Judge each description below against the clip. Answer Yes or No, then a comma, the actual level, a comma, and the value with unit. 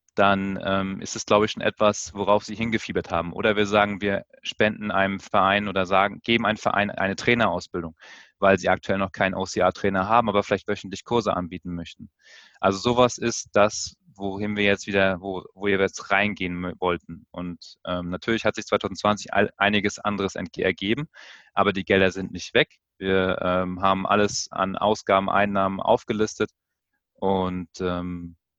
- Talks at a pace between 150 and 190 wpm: Yes, average, 160 wpm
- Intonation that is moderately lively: No, narrow, 1.8 semitones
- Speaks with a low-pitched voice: Yes, very low, 95 Hz